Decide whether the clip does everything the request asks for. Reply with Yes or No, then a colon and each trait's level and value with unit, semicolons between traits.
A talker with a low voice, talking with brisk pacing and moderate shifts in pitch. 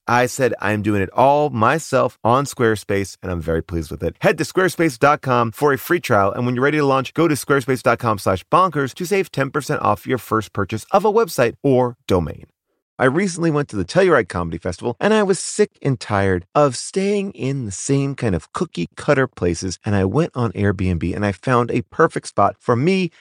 No: low, 125 Hz; fast, 210 wpm; wide, 6.6 semitones